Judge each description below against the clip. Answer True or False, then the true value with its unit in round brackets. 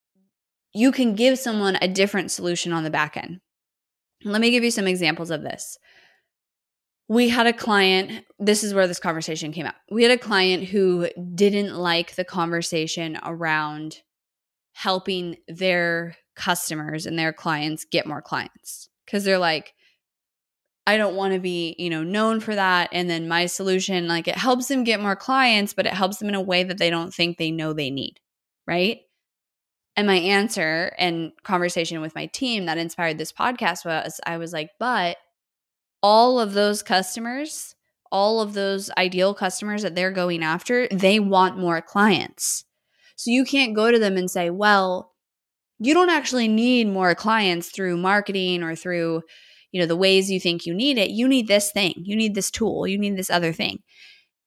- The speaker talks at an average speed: True (180 wpm)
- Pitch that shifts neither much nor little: True (3.6 semitones)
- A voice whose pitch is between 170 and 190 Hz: True (185 Hz)